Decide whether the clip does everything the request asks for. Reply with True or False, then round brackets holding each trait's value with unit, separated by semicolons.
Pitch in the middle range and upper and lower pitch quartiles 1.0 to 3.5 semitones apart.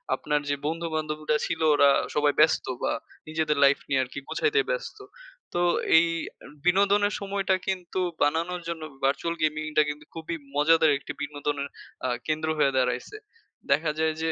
True (155 Hz; 2.5 semitones)